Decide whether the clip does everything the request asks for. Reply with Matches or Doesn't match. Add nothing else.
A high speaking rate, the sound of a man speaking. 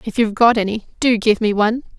Doesn't match